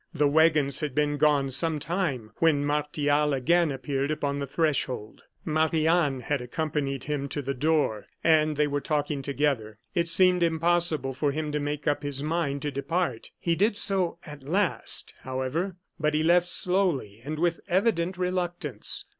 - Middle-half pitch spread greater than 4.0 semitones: No, average, 3.1 semitones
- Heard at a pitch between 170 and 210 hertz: No, medium, 150 Hz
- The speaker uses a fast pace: No, average, 165 wpm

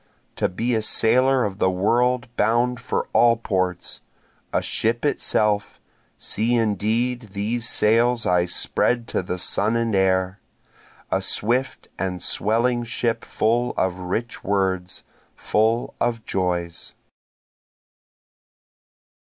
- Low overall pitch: Yes, low, 110 Hz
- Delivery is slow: Yes, slow, 115 wpm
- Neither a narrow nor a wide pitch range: Yes, average, 3.9 semitones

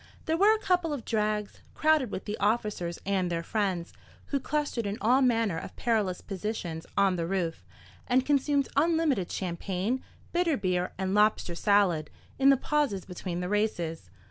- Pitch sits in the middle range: No, high, 210 Hz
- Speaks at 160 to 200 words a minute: Yes, average, 165 wpm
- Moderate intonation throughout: No, wide, 6.9 semitones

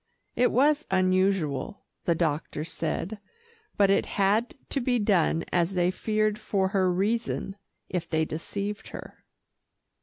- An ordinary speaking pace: No, slow, 130 wpm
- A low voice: No, high, 195 Hz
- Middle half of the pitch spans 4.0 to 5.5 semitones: No, average, 3.5 semitones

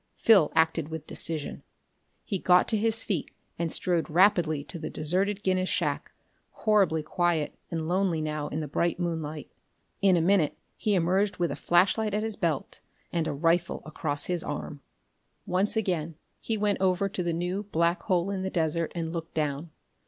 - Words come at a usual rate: Yes, average, 175 wpm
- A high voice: No, medium, 175 Hz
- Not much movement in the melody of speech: No, average, 3.3 semitones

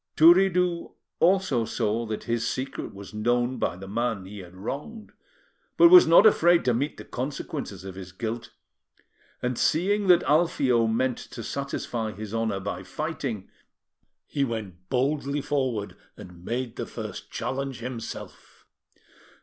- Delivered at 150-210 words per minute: No, average, 140 wpm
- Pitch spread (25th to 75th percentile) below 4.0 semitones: No, average, 5.3 semitones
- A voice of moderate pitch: No, low, 120 Hz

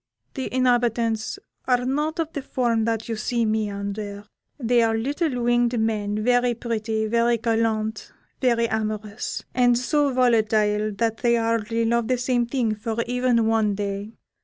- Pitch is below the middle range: No, high, 230 Hz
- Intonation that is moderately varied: No, narrow, 2.1 semitones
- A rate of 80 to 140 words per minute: No, average, 155 wpm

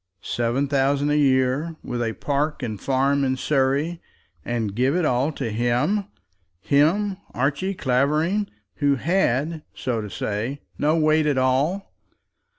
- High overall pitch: No, medium, 140 Hz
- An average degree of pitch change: Yes, average, 3.4 semitones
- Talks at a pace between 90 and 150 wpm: Yes, average, 140 wpm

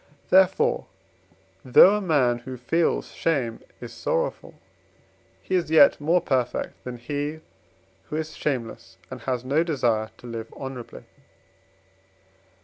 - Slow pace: Yes, slow, 125 wpm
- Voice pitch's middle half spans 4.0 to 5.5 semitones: Yes, average, 4.9 semitones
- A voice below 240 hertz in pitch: Yes, low, 135 Hz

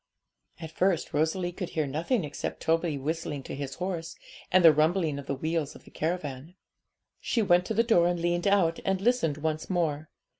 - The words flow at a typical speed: Yes, average, 190 wpm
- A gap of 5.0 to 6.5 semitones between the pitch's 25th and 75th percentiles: No, average, 3.0 semitones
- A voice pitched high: No, medium, 165 Hz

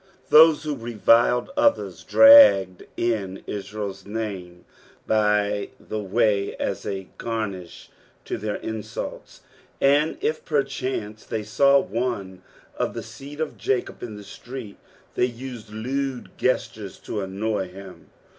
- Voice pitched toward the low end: Yes, low, 110 Hz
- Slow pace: Yes, slow, 125 wpm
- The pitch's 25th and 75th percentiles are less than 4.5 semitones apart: No, average, 4.8 semitones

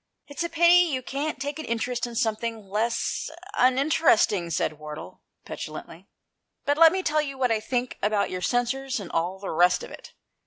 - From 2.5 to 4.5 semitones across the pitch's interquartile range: No, wide, 5.6 semitones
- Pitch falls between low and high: No, high, 245 Hz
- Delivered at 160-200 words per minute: Yes, average, 185 wpm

